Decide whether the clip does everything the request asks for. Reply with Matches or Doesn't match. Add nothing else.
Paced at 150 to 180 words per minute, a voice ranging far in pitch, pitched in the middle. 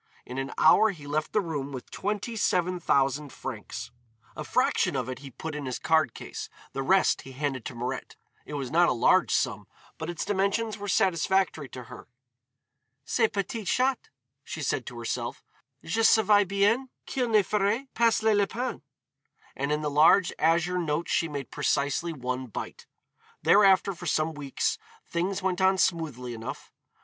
Matches